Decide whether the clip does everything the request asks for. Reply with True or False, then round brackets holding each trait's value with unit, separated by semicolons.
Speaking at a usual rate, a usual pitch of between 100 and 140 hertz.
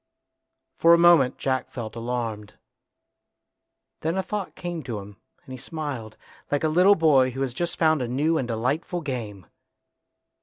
True (160 wpm; 135 Hz)